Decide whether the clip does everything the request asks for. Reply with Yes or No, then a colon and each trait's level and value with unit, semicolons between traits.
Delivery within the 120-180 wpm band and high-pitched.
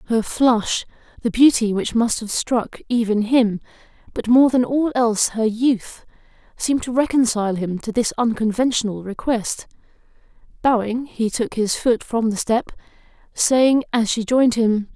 Yes: average, 150 wpm; high, 230 Hz